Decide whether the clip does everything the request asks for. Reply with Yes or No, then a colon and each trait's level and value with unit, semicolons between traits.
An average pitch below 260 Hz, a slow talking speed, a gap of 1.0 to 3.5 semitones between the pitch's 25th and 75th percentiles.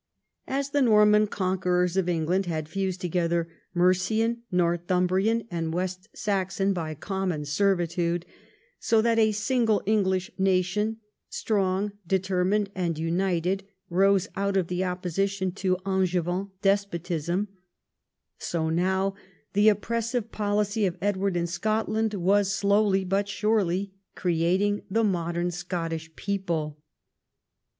Yes: high, 190 Hz; slow, 115 wpm; narrow, 2.6 semitones